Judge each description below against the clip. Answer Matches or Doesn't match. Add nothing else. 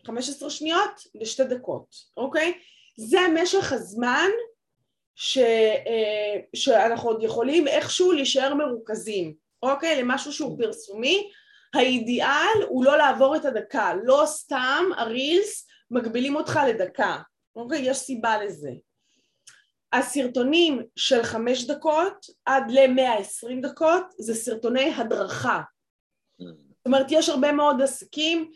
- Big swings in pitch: Doesn't match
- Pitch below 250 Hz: Doesn't match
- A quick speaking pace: Doesn't match